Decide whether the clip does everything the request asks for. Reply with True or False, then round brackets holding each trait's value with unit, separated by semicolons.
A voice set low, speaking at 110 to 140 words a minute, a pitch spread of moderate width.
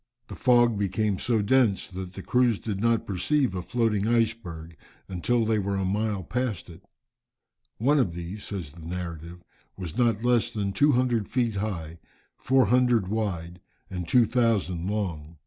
False (105 Hz; 155 wpm; 4.6 semitones)